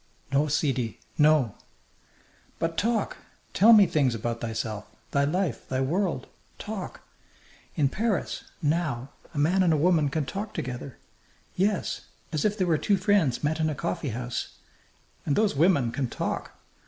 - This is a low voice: No, medium, 155 Hz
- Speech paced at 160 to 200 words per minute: No, average, 150 wpm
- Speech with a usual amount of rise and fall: No, wide, 5.8 semitones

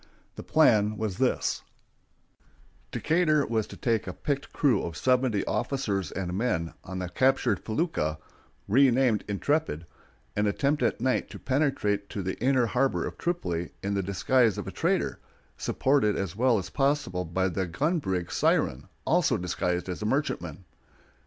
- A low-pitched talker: Yes, low, 110 Hz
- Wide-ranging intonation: Yes, wide, 6.5 semitones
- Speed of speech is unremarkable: Yes, average, 155 wpm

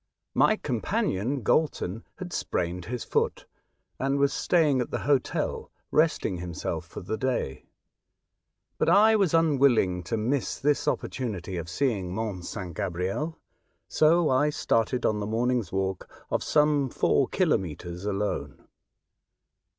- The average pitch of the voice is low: Yes, low, 120 Hz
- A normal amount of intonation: No, wide, 7.4 semitones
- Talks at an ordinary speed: No, slow, 130 wpm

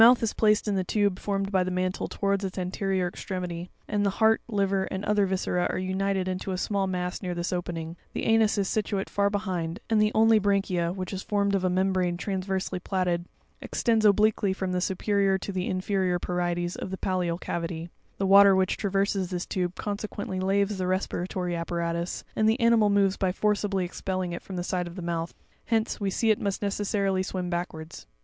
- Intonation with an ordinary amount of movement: No, narrow, 2.0 semitones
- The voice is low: No, high, 190 Hz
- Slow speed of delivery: No, average, 200 wpm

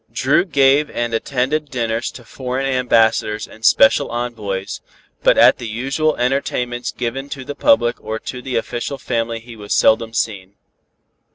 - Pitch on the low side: Yes, low, 120 Hz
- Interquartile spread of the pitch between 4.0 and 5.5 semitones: No, average, 2.9 semitones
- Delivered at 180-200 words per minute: No, average, 155 wpm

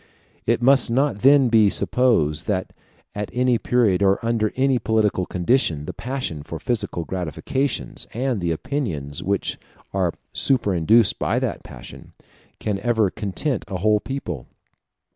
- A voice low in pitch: Yes, low, 110 Hz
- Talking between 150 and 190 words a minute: No, average, 140 wpm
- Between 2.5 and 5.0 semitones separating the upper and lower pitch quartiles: No, wide, 5.4 semitones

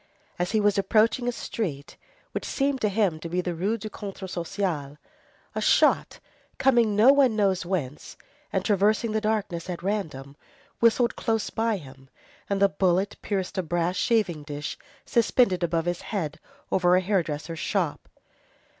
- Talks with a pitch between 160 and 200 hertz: Yes, high, 190 Hz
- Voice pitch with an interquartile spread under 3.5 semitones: No, average, 4.2 semitones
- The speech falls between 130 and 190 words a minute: Yes, average, 160 wpm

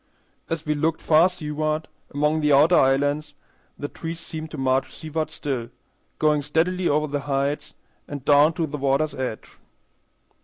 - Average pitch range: No, narrow, 1.7 semitones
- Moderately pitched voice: Yes, medium, 150 Hz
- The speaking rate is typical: Yes, average, 155 wpm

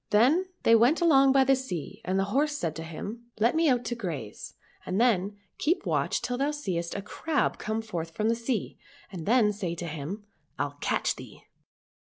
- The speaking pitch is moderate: No, high, 220 Hz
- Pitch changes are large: Yes, wide, 6.3 semitones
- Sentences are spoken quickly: Yes, fast, 210 wpm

